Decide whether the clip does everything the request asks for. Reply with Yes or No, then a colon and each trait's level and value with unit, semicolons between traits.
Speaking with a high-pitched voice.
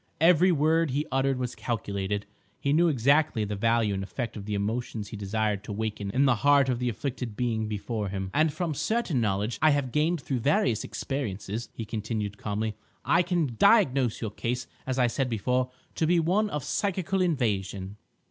No: low, 125 Hz